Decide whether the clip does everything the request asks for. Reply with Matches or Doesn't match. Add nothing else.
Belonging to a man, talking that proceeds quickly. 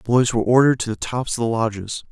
Matches